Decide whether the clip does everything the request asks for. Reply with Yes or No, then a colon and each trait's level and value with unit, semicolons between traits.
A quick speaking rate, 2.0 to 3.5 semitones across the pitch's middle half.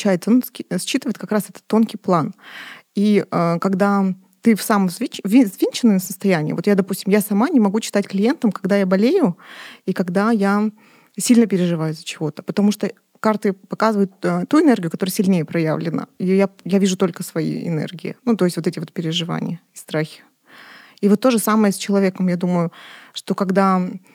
Yes: fast, 170 wpm; average, 2.8 semitones